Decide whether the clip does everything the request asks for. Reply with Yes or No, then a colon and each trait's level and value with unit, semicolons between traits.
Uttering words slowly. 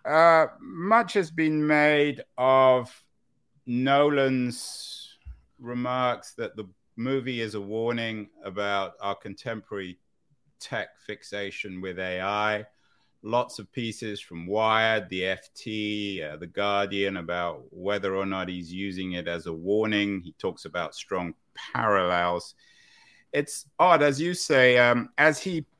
Yes: slow, 125 wpm